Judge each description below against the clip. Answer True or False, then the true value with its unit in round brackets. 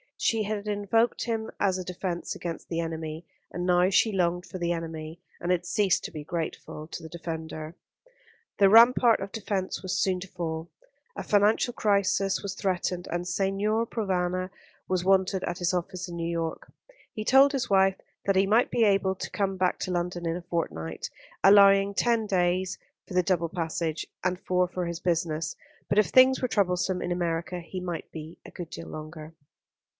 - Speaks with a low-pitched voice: False (180 Hz)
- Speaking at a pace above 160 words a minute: True (185 wpm)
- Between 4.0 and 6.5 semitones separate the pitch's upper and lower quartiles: False (2.6 semitones)